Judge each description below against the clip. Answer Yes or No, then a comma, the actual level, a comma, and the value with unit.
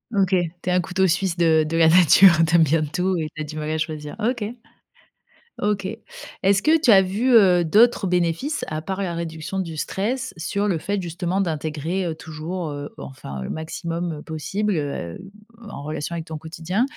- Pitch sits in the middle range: Yes, medium, 170 Hz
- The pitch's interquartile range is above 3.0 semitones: Yes, average, 3.4 semitones